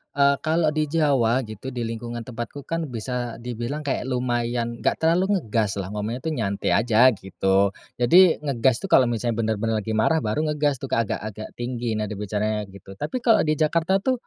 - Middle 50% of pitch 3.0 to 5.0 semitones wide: No, wide, 5.5 semitones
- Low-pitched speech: Yes, low, 120 Hz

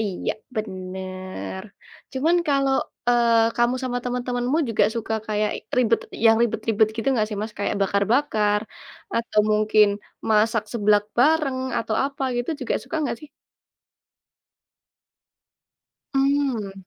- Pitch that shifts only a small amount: No, average, 3.1 semitones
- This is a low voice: No, high, 225 Hz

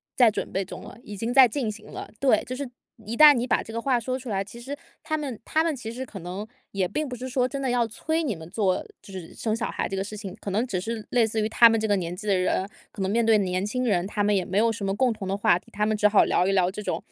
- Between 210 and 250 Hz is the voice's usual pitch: Yes, high, 220 Hz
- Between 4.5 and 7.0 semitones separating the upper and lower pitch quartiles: No, average, 4.0 semitones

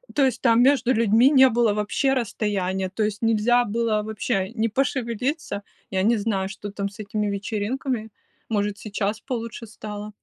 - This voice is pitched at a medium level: No, high, 220 Hz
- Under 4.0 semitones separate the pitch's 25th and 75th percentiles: Yes, average, 2.7 semitones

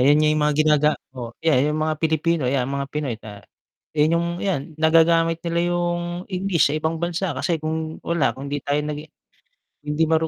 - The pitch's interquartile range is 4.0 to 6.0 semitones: No, narrow, 2.4 semitones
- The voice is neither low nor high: Yes, medium, 155 Hz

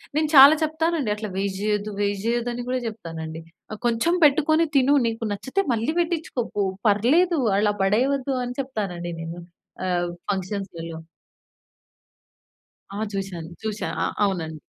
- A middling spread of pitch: No, wide, 6.0 semitones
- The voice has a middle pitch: No, high, 215 Hz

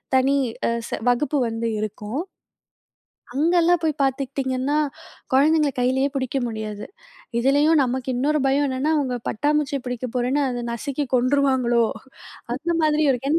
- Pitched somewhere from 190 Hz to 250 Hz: No, very high, 270 Hz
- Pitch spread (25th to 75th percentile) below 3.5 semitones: Yes, average, 2.9 semitones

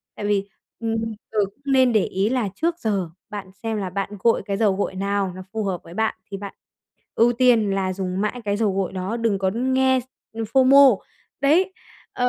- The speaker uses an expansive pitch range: No, average, 4.1 semitones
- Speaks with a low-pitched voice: No, high, 210 Hz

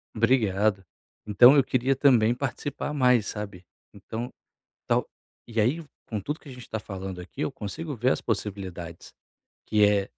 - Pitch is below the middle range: Yes, low, 110 Hz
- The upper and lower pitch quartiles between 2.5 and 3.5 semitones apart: No, average, 4.3 semitones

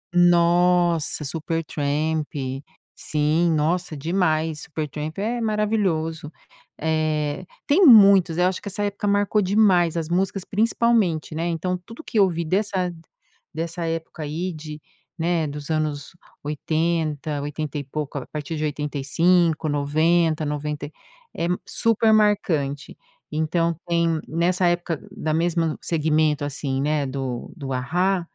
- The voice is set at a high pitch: No, medium, 165 Hz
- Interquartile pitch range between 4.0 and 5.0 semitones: No, average, 3.0 semitones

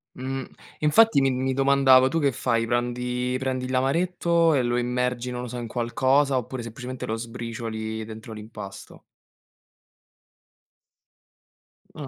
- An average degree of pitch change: No, narrow, 2.2 semitones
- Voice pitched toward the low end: Yes, low, 125 Hz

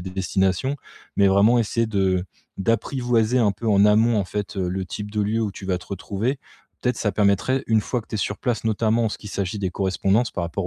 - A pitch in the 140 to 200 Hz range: No, low, 105 Hz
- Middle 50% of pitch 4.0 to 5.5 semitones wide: No, average, 2.9 semitones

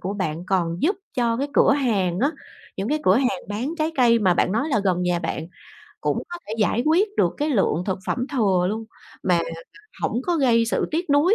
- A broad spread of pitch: Yes, wide, 7.3 semitones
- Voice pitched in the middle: No, high, 230 Hz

